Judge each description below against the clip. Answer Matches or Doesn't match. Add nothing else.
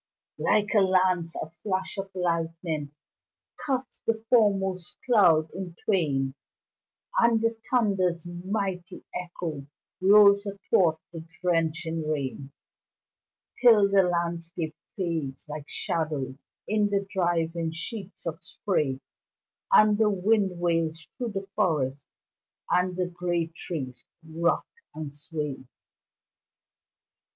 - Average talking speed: Doesn't match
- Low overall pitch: Doesn't match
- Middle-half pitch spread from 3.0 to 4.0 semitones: Matches